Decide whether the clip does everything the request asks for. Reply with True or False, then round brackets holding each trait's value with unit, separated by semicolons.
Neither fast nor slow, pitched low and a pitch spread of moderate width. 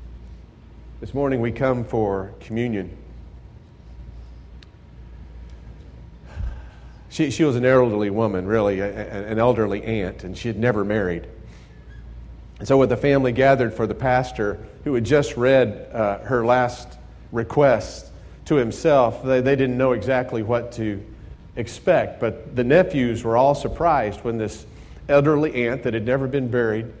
True (145 wpm; 115 Hz; 4.6 semitones)